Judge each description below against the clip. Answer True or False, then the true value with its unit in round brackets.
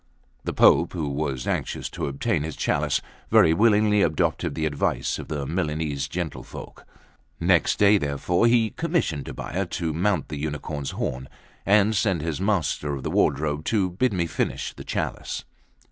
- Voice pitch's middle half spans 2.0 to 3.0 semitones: False (5.3 semitones)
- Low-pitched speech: True (80 Hz)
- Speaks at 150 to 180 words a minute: True (160 wpm)